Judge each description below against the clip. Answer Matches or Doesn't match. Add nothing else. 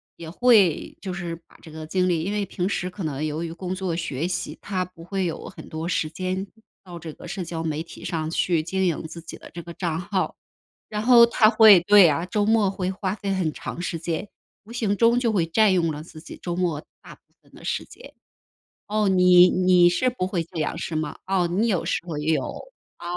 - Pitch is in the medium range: Matches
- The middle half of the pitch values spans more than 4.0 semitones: Doesn't match